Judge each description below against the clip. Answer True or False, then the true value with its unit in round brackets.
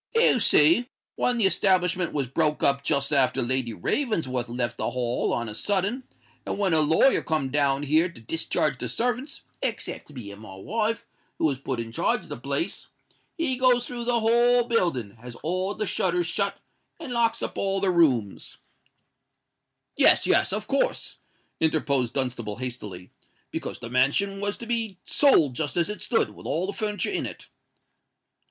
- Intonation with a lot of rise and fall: True (9.0 semitones)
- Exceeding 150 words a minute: True (175 wpm)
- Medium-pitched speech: True (165 Hz)